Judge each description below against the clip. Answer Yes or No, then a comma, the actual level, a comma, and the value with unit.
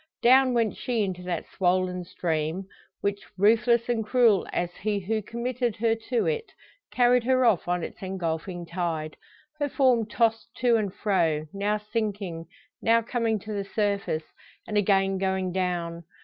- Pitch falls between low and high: No, high, 205 Hz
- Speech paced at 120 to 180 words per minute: Yes, average, 155 wpm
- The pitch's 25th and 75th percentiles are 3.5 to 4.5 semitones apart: Yes, average, 4.2 semitones